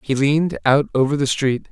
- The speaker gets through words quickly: Yes, fast, 210 wpm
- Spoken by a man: Yes, male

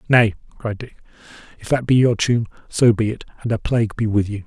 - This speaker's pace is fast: Yes, fast, 230 wpm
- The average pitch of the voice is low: Yes, low, 110 Hz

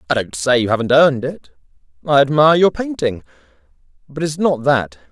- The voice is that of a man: Yes, male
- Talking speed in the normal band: Yes, average, 175 wpm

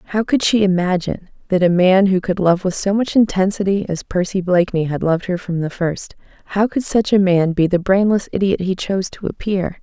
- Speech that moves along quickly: Yes, fast, 215 wpm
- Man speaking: No, female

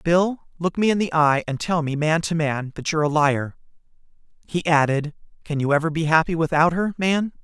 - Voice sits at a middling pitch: Yes, medium, 160 Hz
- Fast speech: Yes, fast, 210 wpm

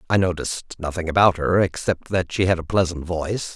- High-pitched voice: No, very low, 90 Hz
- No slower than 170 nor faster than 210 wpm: Yes, average, 200 wpm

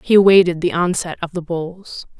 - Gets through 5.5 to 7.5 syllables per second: No, 5.1 syllables/s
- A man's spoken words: No, female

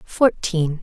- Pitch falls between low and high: Yes, medium, 175 Hz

